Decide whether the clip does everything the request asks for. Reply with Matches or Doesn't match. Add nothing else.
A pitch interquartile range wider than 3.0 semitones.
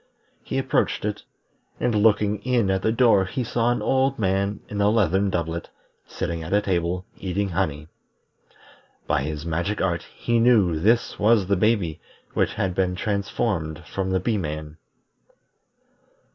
Matches